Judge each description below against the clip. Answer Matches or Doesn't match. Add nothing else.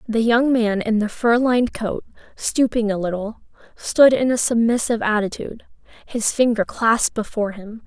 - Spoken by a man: Doesn't match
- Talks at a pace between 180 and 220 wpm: Doesn't match